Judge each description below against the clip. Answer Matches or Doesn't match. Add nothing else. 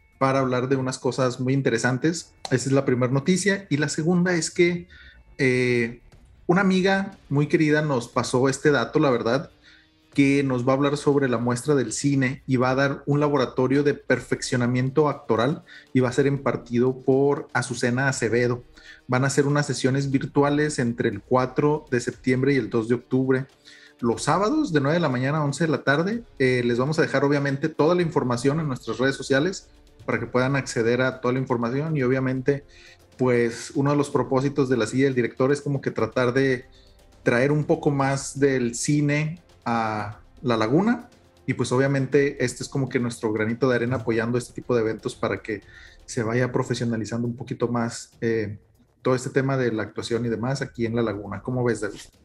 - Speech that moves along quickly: Matches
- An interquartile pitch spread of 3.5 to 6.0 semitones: Doesn't match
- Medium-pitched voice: Doesn't match